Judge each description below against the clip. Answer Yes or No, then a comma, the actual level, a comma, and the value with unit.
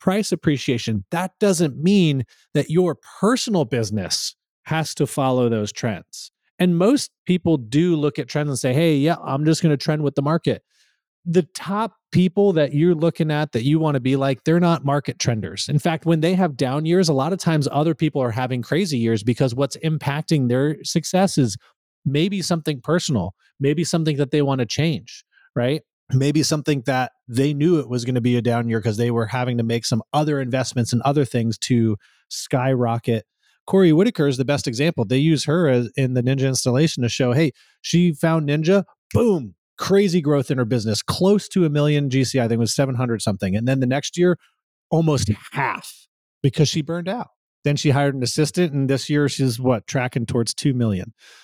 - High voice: No, medium, 145 Hz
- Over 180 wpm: Yes, fast, 205 wpm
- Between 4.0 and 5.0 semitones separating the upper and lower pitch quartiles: Yes, average, 4.6 semitones